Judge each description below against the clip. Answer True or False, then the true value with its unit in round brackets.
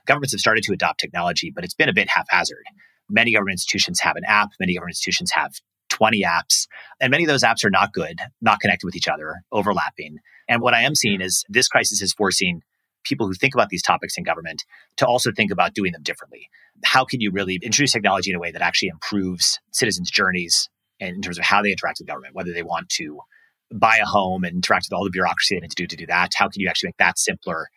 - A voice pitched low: True (90 Hz)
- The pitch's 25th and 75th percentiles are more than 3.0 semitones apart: False (2.5 semitones)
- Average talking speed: False (240 wpm)